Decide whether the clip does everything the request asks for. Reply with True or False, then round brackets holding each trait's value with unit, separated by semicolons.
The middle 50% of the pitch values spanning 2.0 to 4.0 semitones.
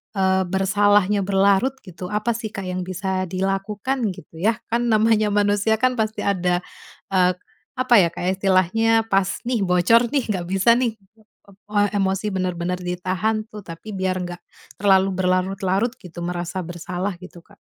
True (2.7 semitones)